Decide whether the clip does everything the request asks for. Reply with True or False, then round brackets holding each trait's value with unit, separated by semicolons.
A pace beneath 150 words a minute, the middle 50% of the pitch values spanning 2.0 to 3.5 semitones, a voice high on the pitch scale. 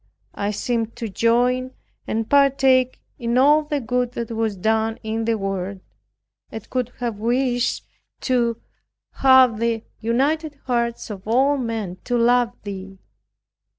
True (135 wpm; 2.4 semitones; 235 Hz)